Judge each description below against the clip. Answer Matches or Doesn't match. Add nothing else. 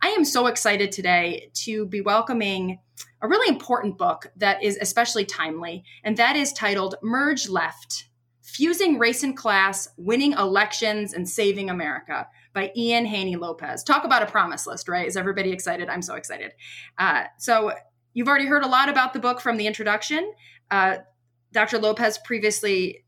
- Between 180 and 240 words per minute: Doesn't match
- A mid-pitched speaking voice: Doesn't match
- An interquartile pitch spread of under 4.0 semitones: Doesn't match